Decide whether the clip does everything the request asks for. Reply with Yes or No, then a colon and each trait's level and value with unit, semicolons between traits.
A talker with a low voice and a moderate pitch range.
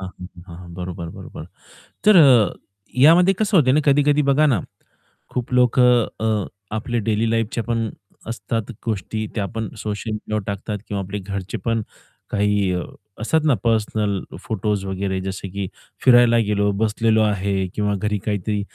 Yes: low, 110 Hz; average, 3.0 semitones